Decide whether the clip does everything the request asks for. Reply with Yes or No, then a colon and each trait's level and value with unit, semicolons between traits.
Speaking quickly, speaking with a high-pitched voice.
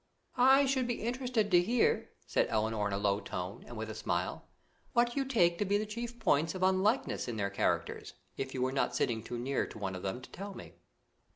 No: fast, 225 wpm; medium, 175 Hz